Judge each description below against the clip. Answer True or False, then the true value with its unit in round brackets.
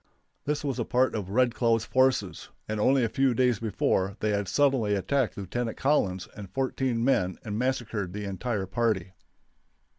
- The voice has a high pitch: False (115 Hz)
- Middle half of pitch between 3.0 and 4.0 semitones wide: False (4.4 semitones)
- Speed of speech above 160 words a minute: True (170 wpm)